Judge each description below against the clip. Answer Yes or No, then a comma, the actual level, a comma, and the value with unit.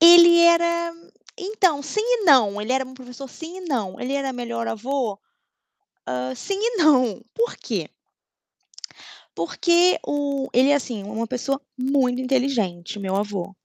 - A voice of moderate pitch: No, very high, 265 Hz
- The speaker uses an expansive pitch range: Yes, wide, 6.7 semitones